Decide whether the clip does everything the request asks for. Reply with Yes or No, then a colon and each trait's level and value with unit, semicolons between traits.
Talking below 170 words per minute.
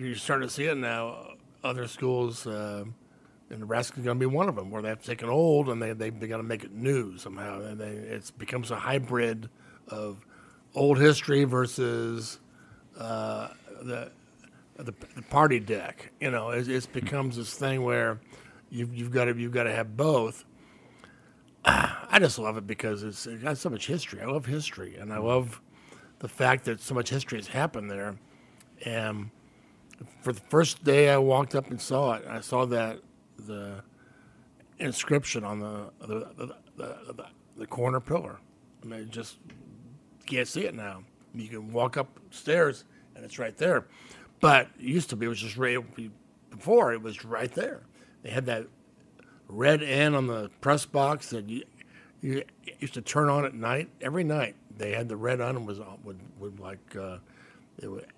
No: average, 185 wpm